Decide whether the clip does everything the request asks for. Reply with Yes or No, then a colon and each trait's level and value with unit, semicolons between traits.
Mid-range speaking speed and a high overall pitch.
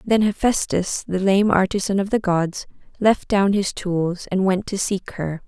Yes: average, 185 wpm; high, 195 Hz